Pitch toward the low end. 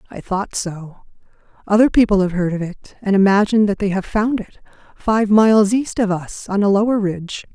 No: high, 205 Hz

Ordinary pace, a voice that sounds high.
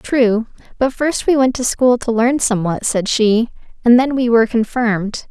Yes: average, 190 wpm; high, 235 Hz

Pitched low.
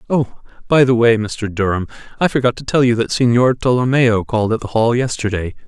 Yes: low, 120 Hz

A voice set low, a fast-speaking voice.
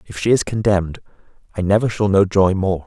Yes: low, 100 Hz; fast, 210 wpm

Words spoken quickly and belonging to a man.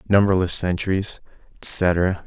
No: slow, 80 wpm; male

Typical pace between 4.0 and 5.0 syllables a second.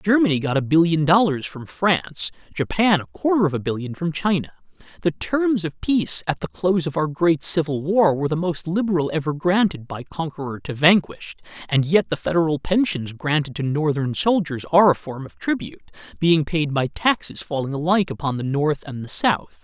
No: 5.4 syllables/s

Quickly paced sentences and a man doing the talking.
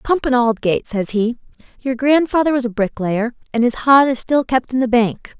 No: fast, 210 wpm; female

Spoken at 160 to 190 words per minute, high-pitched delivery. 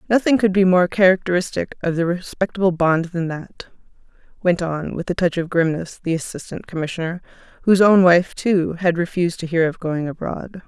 No: average, 180 wpm; medium, 175 Hz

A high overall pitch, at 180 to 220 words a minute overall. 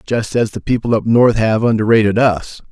No: low, 110 Hz; average, 200 wpm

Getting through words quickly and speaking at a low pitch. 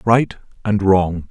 No: average, 140 wpm; low, 100 Hz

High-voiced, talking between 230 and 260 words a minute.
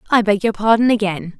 No: high, 210 Hz; fast, 215 wpm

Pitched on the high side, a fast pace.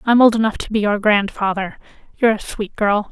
Yes: high, 210 Hz; fast, 210 wpm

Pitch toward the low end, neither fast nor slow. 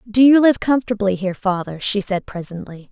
No: high, 210 Hz; average, 185 wpm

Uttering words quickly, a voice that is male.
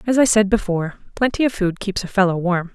No: fast, 240 wpm; female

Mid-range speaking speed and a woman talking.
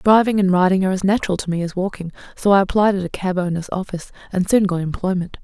No: fast, 230 wpm; female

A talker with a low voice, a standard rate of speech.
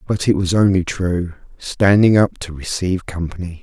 Yes: very low, 90 Hz; average, 165 wpm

